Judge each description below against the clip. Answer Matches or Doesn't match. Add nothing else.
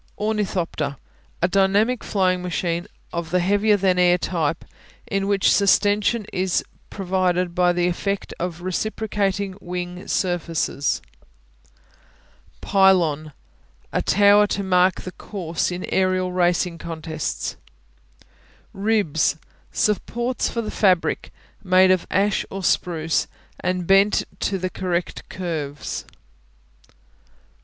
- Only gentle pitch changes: Matches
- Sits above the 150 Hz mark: Matches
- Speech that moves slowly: Matches